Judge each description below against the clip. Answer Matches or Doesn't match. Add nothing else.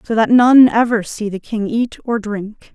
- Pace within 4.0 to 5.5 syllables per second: Matches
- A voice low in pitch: Doesn't match